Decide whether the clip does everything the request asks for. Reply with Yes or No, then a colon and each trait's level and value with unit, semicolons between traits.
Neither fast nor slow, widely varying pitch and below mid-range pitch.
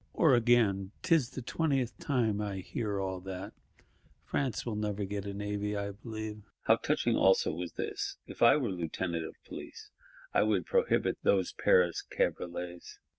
Yes: average, 160 wpm; wide, 5.8 semitones; low, 105 Hz